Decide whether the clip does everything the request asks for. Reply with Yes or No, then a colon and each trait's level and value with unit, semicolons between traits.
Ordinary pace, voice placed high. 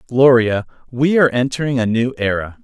No: average, 160 wpm; low, 125 Hz